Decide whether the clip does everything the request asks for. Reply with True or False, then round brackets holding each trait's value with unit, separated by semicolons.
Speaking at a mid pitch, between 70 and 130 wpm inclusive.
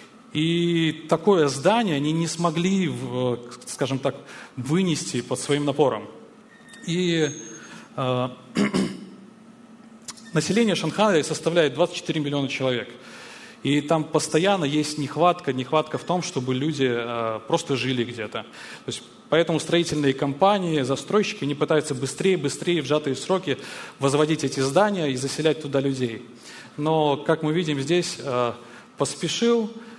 True (155 Hz; 120 wpm)